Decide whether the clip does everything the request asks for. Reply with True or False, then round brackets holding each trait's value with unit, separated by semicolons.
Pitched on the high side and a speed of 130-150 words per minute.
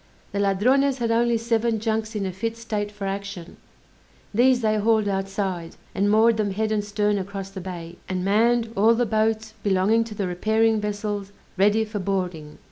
False (210 Hz; 180 wpm)